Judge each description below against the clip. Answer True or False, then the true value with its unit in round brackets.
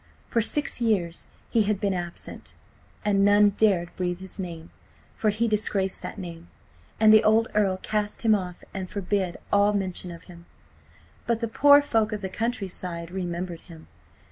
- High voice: True (195 Hz)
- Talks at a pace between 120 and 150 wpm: False (170 wpm)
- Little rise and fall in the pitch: False (3.3 semitones)